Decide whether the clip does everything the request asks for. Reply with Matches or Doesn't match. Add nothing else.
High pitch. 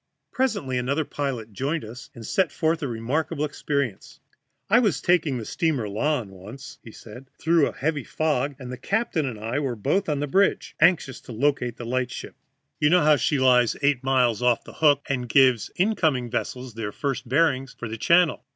Doesn't match